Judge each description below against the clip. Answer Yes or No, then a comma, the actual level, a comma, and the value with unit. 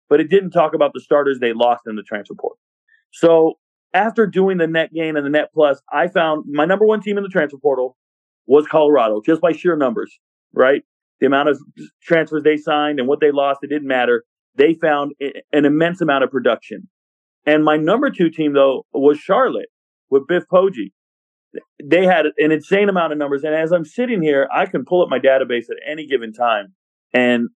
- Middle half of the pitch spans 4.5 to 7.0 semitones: No, average, 3.7 semitones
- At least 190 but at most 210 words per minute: Yes, fast, 205 wpm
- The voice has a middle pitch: Yes, medium, 150 Hz